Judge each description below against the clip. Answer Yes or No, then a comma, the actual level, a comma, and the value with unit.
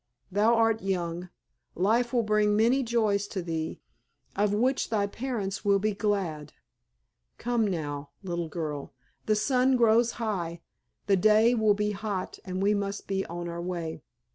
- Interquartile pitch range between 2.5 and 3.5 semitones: No, average, 3.9 semitones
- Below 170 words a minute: Yes, average, 155 wpm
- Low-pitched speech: No, high, 205 Hz